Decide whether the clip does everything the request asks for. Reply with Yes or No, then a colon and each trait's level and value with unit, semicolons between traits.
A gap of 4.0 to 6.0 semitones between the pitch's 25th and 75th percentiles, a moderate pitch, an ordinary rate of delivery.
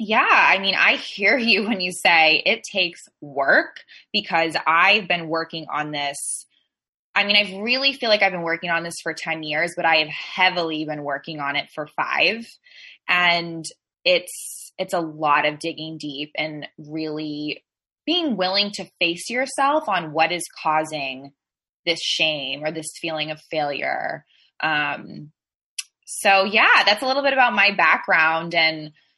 Yes: average, 4.7 semitones; medium, 165 Hz; average, 160 wpm